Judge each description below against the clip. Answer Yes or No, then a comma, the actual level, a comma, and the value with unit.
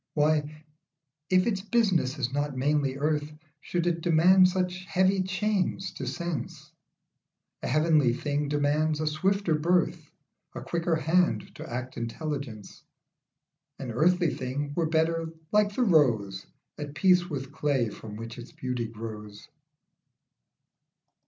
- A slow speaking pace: Yes, slow, 130 wpm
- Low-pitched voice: No, medium, 155 Hz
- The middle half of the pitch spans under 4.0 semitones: No, average, 5.0 semitones